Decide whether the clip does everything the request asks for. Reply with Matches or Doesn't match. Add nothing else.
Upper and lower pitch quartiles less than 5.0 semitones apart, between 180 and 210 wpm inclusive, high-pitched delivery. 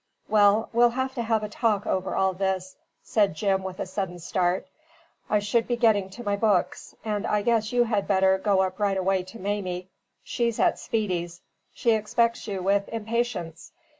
Matches